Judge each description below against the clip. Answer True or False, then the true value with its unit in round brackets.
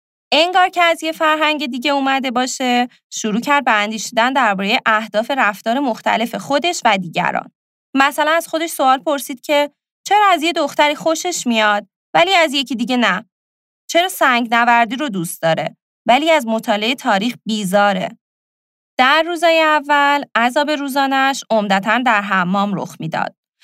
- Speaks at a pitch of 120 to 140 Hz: False (260 Hz)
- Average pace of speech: True (145 wpm)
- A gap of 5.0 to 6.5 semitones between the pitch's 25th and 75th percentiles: True (5.5 semitones)